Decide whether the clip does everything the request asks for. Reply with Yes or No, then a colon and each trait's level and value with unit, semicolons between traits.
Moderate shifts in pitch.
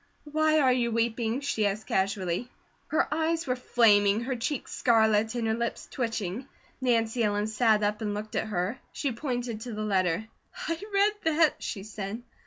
Yes: average, 3.4 semitones